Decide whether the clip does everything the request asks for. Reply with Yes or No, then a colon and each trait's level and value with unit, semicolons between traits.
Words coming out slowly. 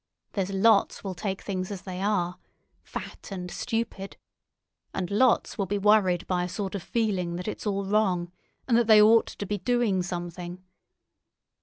No: average, 165 wpm